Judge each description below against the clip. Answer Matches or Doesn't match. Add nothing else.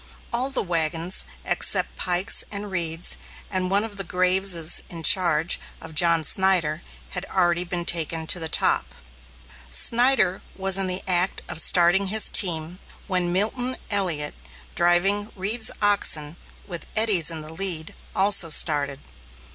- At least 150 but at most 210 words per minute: Doesn't match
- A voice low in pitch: Doesn't match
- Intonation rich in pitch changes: Doesn't match